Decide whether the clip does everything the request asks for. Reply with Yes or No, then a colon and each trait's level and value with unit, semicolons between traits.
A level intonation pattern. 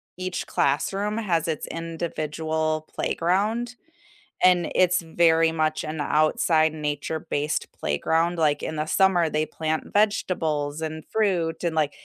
Yes: narrow, 2.3 semitones